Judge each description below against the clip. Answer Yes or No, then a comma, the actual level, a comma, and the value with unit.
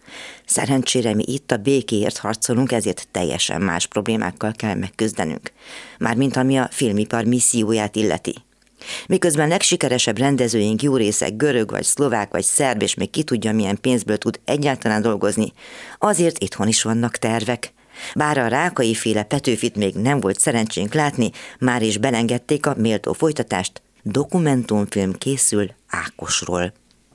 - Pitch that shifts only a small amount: No, average, 4.0 semitones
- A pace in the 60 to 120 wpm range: No, average, 135 wpm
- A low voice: Yes, low, 115 Hz